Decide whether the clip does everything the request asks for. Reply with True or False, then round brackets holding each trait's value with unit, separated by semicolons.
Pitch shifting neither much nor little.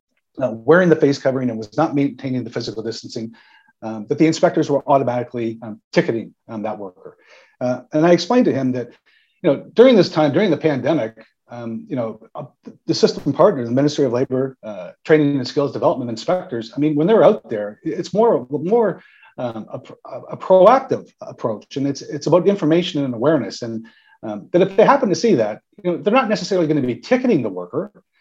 False (5.8 semitones)